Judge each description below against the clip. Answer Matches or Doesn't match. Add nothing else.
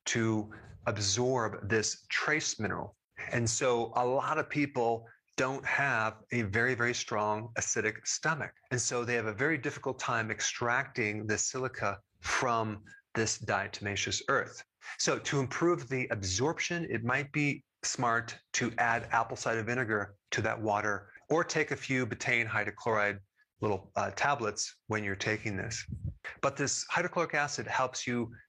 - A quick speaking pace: Doesn't match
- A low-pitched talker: Matches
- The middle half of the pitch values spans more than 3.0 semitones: Matches